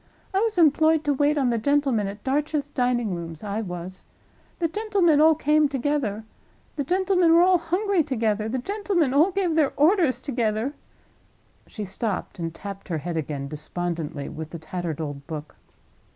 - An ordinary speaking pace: Yes, average, 165 wpm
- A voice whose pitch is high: Yes, very high, 260 Hz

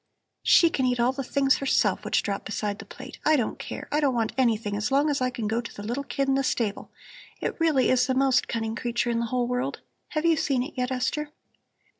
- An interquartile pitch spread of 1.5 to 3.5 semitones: Yes, average, 2.9 semitones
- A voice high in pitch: Yes, very high, 255 Hz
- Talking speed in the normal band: No, fast, 245 wpm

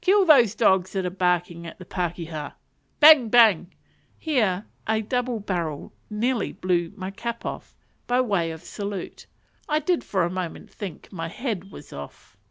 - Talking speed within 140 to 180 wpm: Yes, average, 165 wpm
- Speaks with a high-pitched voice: Yes, high, 195 Hz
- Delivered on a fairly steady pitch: No, average, 5.1 semitones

